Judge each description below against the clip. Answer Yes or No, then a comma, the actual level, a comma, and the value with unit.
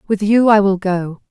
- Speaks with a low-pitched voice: No, high, 200 Hz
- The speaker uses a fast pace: Yes, fast, 230 wpm